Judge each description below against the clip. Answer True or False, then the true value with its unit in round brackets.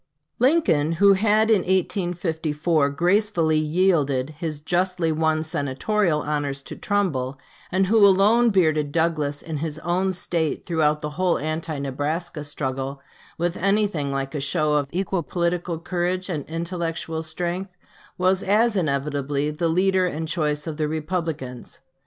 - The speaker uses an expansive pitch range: False (3.6 semitones)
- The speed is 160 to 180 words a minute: False (140 wpm)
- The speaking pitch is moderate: True (165 Hz)